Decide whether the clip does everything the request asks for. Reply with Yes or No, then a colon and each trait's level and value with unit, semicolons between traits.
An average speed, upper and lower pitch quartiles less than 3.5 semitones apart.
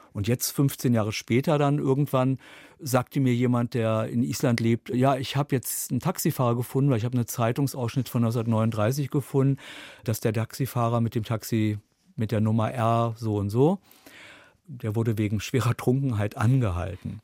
Yes: average, 165 wpm; average, 3.1 semitones